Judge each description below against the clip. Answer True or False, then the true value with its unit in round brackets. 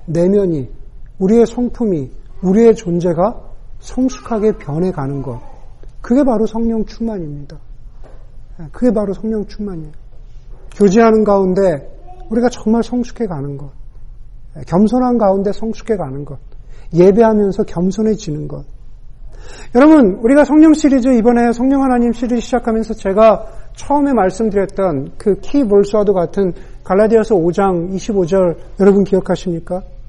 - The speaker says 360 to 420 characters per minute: False (295 characters per minute)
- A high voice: True (195 Hz)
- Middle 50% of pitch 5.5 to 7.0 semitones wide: False (7.7 semitones)